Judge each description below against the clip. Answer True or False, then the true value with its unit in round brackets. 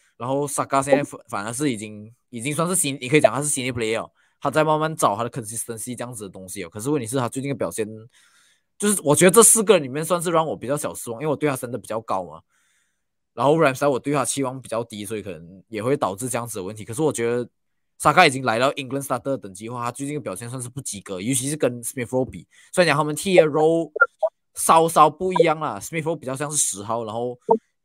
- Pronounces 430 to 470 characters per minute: True (455 characters per minute)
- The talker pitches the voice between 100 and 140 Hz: True (135 Hz)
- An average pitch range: True (4.7 semitones)